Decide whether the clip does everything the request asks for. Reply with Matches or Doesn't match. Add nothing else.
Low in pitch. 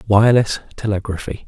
Matches